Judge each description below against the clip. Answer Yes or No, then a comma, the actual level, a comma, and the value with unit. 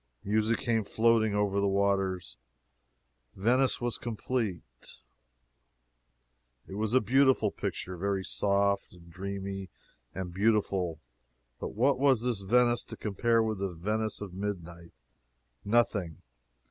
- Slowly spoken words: Yes, slow, 120 wpm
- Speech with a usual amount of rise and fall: Yes, average, 3.1 semitones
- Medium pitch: No, low, 100 Hz